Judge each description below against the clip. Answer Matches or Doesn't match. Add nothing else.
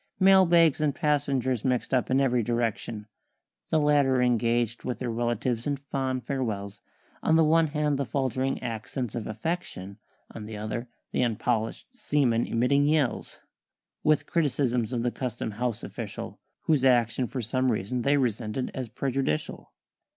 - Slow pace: Doesn't match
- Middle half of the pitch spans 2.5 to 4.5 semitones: Matches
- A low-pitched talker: Matches